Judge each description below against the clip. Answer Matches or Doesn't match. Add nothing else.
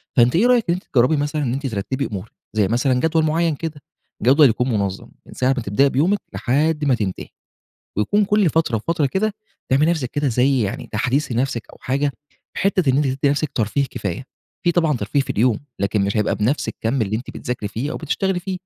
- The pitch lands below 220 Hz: Matches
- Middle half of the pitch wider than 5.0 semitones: Matches